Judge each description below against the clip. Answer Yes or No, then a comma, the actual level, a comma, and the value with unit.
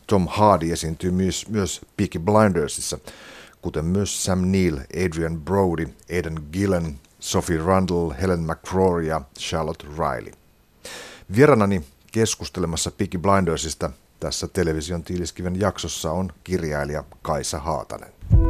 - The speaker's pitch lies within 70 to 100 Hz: Yes, very low, 85 Hz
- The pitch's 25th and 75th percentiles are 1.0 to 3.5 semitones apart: Yes, average, 2.8 semitones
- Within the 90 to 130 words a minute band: Yes, average, 110 wpm